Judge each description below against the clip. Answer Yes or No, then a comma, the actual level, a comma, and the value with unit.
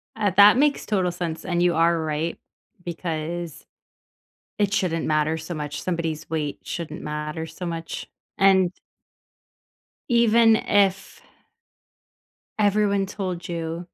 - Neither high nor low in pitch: Yes, medium, 175 Hz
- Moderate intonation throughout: Yes, average, 3.3 semitones